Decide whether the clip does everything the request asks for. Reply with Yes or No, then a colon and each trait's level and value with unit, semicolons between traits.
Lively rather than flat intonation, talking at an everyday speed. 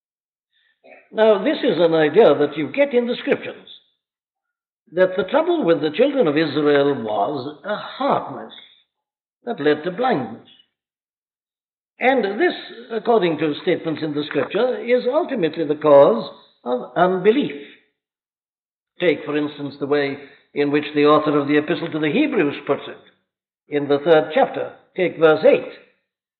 Yes: wide, 8.7 semitones; average, 145 wpm